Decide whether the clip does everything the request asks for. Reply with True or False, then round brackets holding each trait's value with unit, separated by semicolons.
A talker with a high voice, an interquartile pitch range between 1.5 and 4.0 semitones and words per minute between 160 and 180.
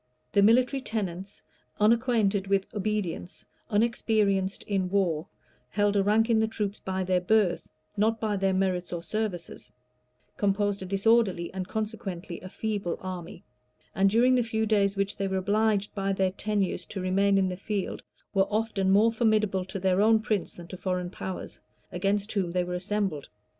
True (200 Hz; 2.4 semitones; 170 wpm)